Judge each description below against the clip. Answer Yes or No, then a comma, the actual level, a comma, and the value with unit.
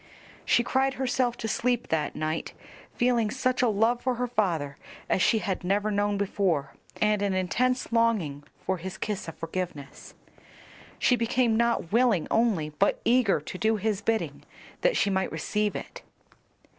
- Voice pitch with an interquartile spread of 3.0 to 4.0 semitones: No, average, 4.4 semitones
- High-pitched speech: Yes, high, 210 Hz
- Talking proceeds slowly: No, average, 160 wpm